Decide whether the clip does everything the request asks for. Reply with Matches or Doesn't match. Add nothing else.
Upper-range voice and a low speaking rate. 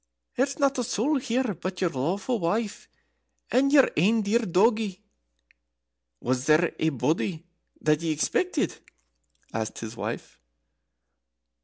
Matches